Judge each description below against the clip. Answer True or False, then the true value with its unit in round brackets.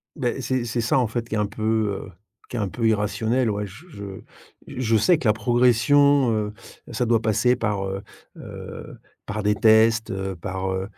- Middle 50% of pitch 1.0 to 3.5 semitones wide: True (2.7 semitones)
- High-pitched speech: False (110 Hz)